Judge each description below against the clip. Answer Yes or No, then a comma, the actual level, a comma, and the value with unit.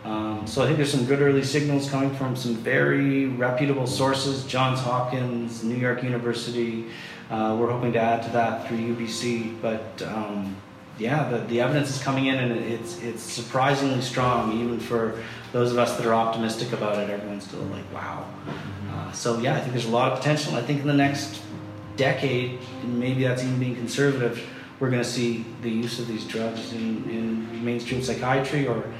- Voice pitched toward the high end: No, low, 120 Hz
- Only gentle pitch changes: Yes, narrow, 2.3 semitones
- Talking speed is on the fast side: No, average, 190 wpm